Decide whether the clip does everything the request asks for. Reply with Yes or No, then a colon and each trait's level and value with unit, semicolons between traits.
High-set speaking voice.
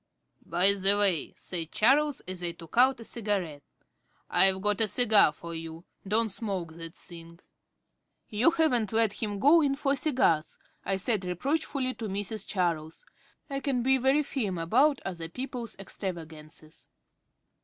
Yes: high, 205 Hz